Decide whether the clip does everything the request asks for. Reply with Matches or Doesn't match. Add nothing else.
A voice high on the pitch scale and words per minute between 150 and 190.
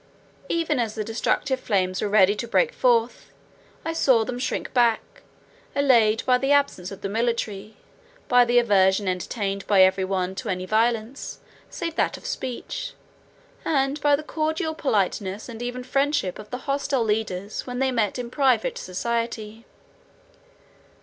Matches